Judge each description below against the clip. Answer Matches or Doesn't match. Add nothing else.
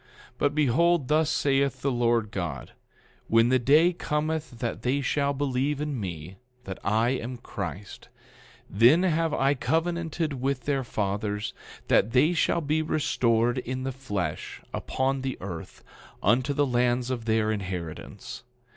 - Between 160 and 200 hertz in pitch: Doesn't match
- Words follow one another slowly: Doesn't match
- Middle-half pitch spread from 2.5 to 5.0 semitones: Matches